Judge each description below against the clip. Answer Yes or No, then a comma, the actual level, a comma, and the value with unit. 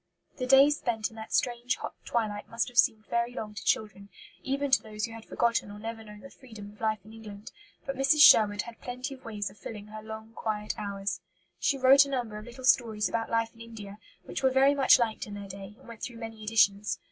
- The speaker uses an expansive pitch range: No, average, 2.8 semitones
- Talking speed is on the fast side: Yes, fast, 235 wpm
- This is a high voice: Yes, high, 225 Hz